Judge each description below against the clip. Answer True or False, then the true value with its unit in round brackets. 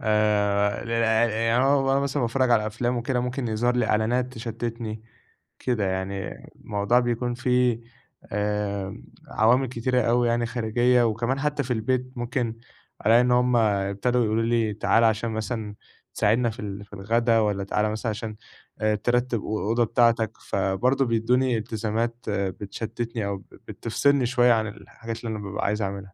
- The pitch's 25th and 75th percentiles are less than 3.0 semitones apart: True (2.5 semitones)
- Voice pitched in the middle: False (115 Hz)